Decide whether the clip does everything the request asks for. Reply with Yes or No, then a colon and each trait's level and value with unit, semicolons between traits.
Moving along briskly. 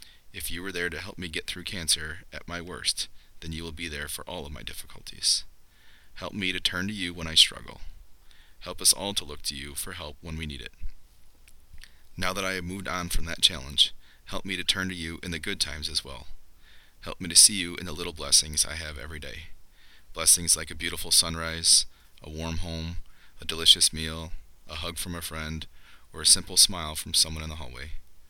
Yes: fast, 220 wpm